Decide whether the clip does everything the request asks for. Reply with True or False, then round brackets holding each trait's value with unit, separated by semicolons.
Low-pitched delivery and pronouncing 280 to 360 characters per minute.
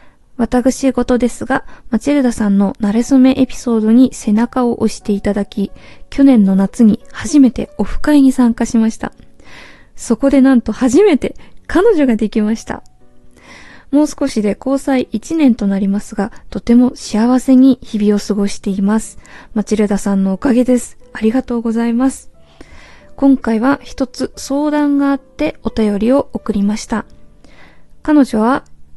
False (235 Hz; 295 characters per minute)